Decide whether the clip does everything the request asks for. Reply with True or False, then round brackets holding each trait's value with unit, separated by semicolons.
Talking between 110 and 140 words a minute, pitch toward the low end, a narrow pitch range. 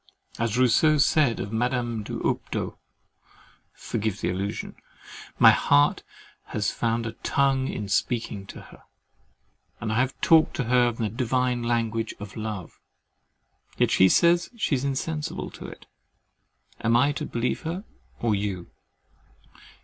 False (135 wpm; 120 Hz; 3.8 semitones)